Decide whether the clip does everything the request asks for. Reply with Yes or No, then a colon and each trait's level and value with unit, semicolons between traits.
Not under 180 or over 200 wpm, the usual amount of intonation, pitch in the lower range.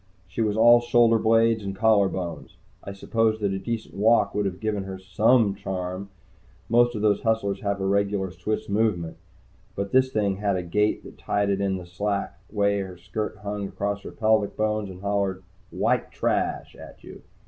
No: average, 185 wpm; narrow, 2.2 semitones; low, 100 Hz